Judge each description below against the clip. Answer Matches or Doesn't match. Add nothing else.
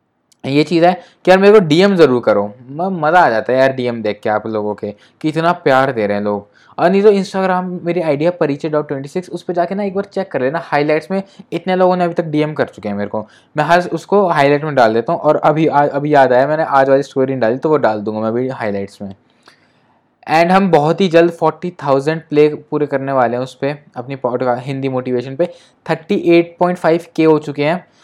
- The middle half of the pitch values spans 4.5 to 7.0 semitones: Matches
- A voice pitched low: Doesn't match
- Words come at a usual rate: Doesn't match